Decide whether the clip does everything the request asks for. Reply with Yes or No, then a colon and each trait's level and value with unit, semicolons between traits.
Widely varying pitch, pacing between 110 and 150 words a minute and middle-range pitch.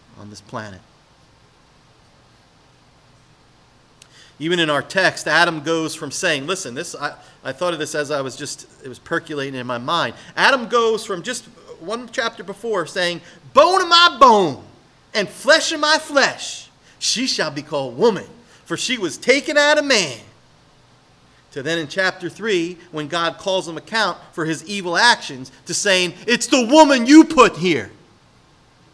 No: wide, 7.7 semitones; average, 165 wpm; medium, 180 Hz